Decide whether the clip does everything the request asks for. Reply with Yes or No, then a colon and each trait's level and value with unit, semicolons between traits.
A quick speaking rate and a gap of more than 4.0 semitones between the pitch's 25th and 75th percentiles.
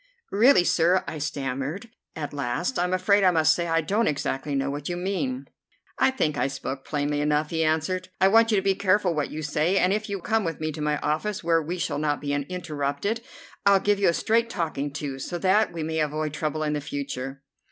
Yes: fast, 225 wpm; average, 4.7 semitones